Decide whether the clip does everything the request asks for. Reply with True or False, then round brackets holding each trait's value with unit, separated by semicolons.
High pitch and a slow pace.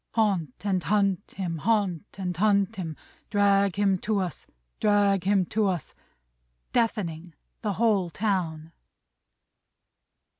True (195 Hz; 115 wpm)